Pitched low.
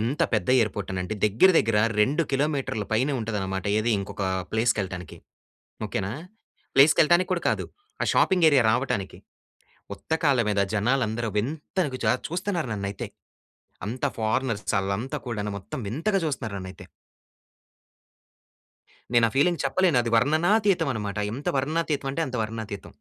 Yes: low, 120 Hz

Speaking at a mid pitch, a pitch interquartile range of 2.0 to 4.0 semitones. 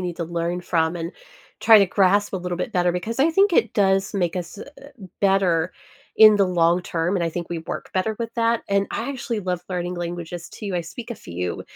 Yes: medium, 180 Hz; average, 3.0 semitones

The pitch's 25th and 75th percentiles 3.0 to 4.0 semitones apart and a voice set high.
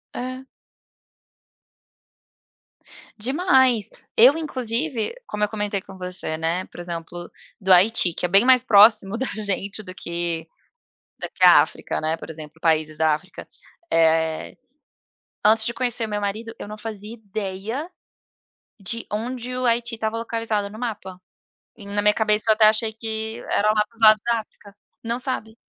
Yes: average, 3.5 semitones; high, 215 Hz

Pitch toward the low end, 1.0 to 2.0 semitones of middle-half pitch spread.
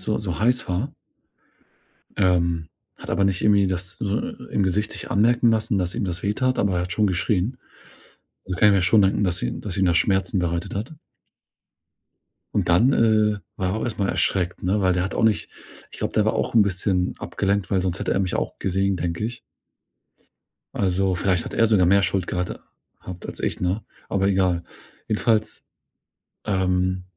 No: very low, 95 Hz; narrow, 2.6 semitones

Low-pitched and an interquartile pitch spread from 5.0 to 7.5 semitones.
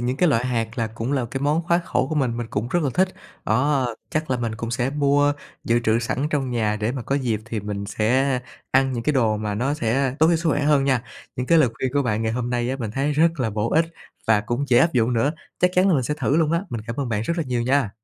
No: low, 130 Hz; average, 3.9 semitones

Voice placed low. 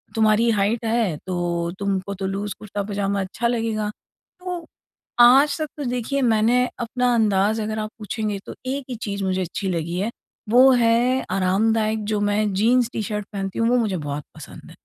No: high, 215 Hz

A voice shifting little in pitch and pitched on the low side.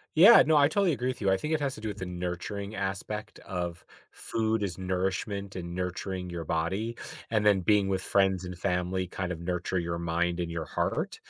No: average, 3.1 semitones; very low, 95 Hz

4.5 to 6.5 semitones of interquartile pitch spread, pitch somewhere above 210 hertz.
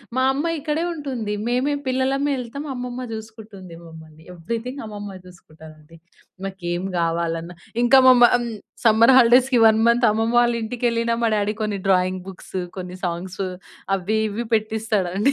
Yes: average, 4.9 semitones; high, 220 Hz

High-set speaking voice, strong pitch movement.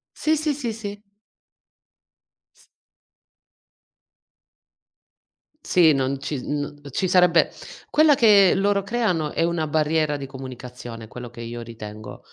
No: medium, 155 Hz; wide, 7.7 semitones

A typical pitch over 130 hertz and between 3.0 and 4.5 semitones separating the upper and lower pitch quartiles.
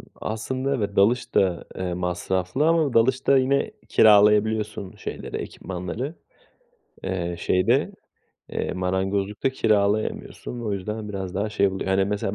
No: low, 105 Hz; average, 4.1 semitones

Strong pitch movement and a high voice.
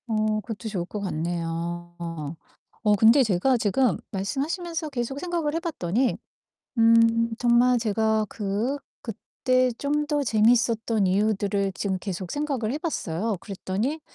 No: average, 4.7 semitones; high, 220 Hz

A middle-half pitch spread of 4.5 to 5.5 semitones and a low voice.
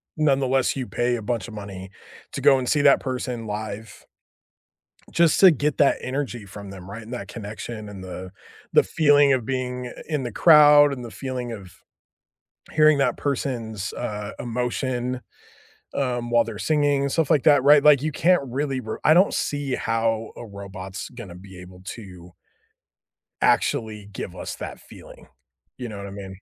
Yes: average, 5.0 semitones; low, 120 Hz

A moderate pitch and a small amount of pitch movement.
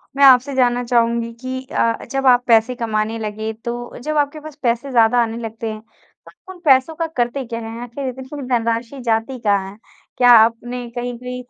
No: high, 240 Hz; narrow, 2.2 semitones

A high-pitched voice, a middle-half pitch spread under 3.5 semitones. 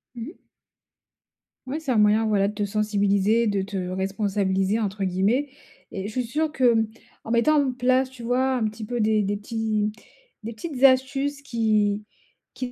No: high, 220 Hz; average, 3.8 semitones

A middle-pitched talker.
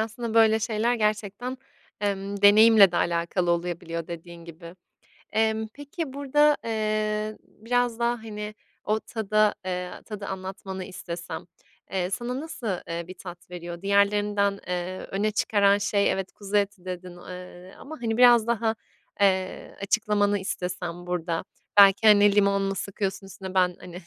No: high, 200 Hz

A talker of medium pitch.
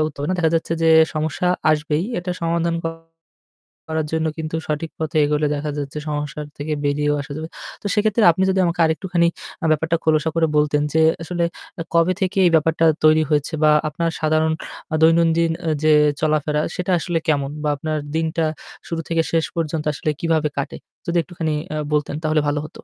Yes: medium, 160 Hz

